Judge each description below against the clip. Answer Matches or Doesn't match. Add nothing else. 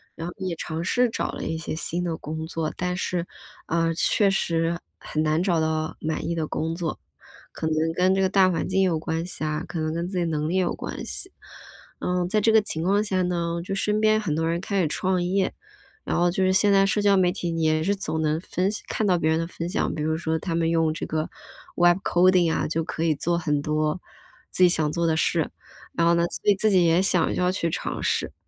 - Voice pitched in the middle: Matches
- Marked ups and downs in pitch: Doesn't match